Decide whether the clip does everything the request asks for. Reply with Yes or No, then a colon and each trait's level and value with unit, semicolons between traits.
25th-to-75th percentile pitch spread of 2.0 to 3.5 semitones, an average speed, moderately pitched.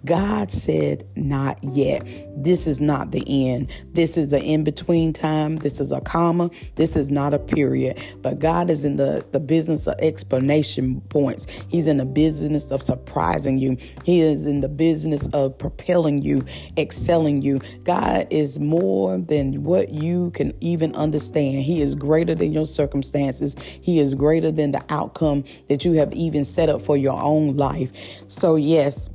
Yes: average, 2.7 semitones; average, 170 wpm; medium, 145 Hz